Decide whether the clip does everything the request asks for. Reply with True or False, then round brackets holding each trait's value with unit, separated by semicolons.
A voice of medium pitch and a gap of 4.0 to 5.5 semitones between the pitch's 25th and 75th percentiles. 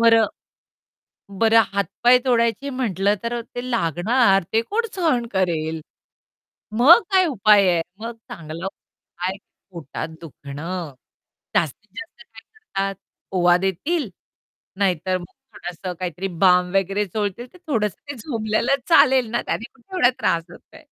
False (210 Hz; 5.1 semitones)